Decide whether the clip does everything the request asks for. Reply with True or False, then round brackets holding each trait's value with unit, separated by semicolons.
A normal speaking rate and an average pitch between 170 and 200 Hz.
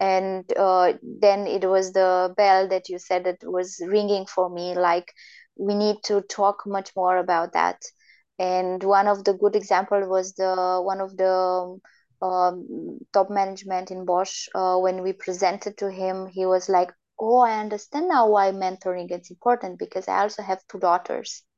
True (175 wpm; 190 Hz)